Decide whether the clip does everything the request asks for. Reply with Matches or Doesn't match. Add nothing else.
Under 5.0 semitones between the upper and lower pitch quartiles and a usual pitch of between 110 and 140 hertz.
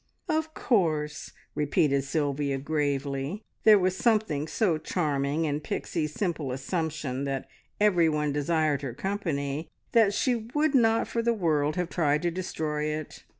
Doesn't match